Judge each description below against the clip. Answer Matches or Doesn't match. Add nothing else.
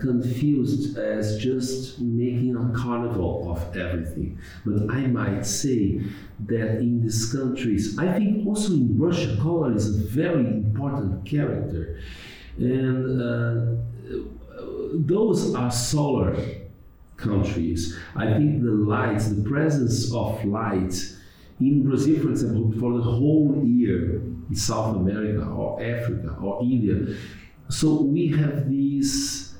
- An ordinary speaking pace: Doesn't match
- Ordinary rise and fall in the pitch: Matches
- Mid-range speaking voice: Doesn't match